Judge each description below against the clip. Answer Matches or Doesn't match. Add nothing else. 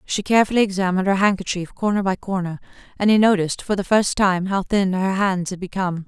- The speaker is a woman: Matches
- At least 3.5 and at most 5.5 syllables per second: Doesn't match